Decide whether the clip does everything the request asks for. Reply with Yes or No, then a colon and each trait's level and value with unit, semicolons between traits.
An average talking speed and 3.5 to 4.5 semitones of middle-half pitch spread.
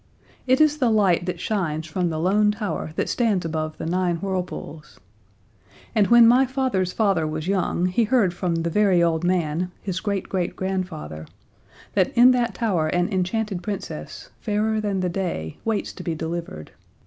Yes: average, 170 wpm; average, 4.0 semitones